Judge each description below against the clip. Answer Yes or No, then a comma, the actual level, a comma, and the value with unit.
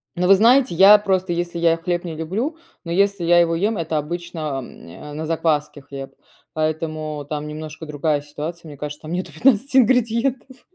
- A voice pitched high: No, medium, 170 Hz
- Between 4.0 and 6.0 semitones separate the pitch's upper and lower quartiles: Yes, average, 4.3 semitones